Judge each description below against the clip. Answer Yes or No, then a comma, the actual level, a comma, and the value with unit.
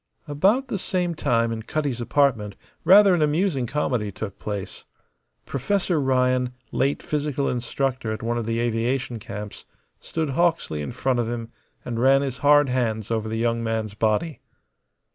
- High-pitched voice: No, low, 125 Hz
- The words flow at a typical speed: Yes, average, 160 wpm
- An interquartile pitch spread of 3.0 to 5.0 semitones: Yes, average, 4.5 semitones